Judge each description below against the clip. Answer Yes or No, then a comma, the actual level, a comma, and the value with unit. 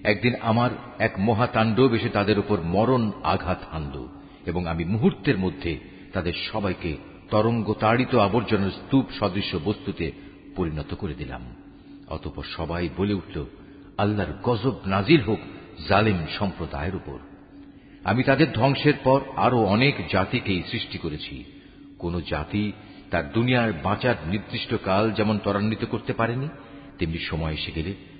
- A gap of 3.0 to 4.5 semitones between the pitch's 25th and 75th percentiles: No, average, 5.1 semitones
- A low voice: Yes, low, 105 Hz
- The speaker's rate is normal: No, fast, 125 wpm